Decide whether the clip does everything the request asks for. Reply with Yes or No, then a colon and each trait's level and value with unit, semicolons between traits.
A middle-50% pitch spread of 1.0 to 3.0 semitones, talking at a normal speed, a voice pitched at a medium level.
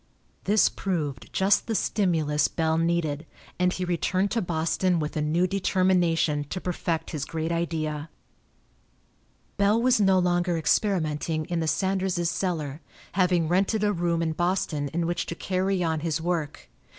Yes: average, 2.7 semitones; average, 150 wpm; medium, 170 Hz